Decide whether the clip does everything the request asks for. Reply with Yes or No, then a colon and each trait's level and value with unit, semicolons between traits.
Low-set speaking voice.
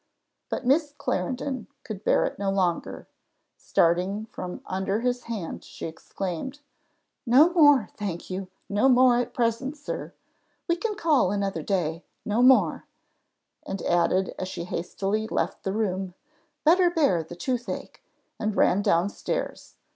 No: high, 210 Hz